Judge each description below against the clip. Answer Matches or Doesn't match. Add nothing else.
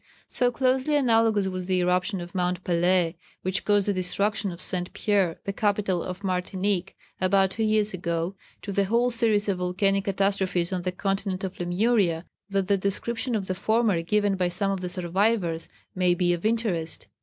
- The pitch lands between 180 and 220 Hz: Matches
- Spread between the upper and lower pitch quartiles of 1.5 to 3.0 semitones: Matches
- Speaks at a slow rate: Doesn't match